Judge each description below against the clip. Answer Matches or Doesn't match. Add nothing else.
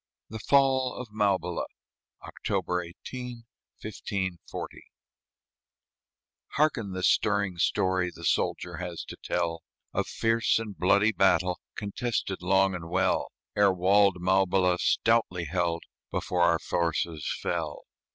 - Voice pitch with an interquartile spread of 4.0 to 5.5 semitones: Doesn't match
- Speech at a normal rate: Doesn't match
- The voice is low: Matches